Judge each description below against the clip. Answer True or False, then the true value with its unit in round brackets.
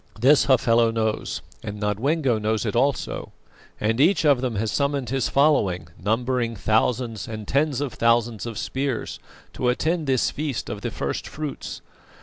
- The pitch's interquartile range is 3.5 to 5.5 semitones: True (3.9 semitones)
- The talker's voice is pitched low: True (120 Hz)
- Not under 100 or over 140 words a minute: False (155 wpm)